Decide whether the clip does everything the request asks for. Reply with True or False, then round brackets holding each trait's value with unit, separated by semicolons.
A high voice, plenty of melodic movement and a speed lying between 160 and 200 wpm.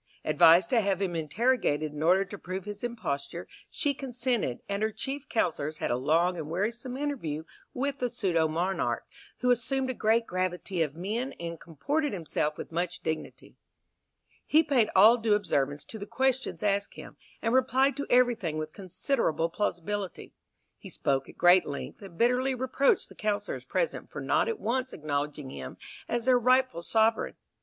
True (205 Hz; 6.9 semitones; 170 wpm)